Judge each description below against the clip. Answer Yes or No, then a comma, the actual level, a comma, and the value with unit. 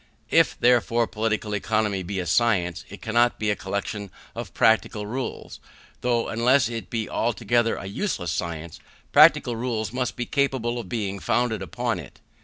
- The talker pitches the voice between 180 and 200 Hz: No, low, 110 Hz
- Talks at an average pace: Yes, average, 160 wpm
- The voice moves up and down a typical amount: Yes, average, 3.0 semitones